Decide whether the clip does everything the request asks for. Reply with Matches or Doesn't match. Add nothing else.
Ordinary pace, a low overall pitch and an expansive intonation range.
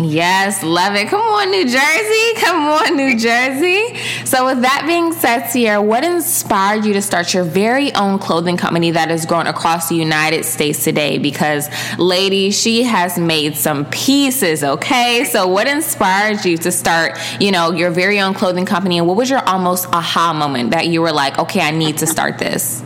Doesn't match